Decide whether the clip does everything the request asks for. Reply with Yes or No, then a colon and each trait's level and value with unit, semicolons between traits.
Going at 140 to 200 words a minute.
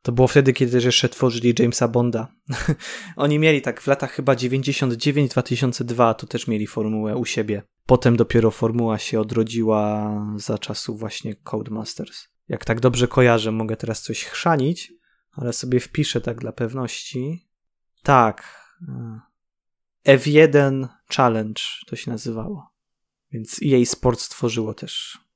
No: average, 130 wpm